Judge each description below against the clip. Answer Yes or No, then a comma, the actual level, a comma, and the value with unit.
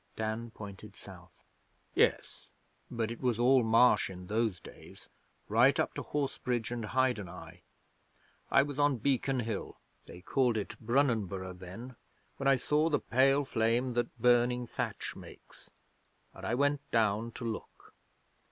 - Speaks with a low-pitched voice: Yes, low, 115 Hz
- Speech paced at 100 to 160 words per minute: Yes, average, 145 wpm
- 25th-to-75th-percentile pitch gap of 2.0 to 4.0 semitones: Yes, average, 3.5 semitones